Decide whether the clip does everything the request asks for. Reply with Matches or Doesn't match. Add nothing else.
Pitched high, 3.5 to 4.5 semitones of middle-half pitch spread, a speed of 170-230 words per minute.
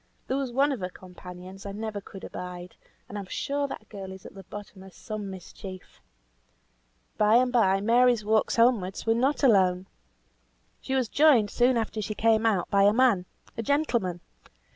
Matches